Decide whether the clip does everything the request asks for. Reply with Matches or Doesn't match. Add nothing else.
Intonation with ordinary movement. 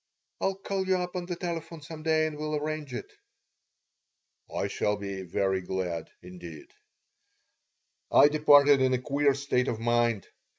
Doesn't match